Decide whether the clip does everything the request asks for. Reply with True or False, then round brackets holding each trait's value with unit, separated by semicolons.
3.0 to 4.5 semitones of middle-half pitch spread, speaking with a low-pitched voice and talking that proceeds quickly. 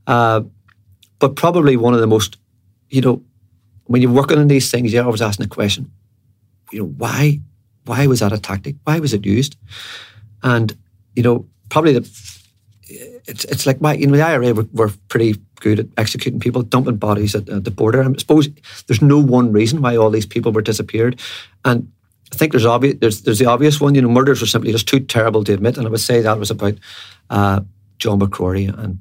True (3.6 semitones; 115 Hz; 210 wpm)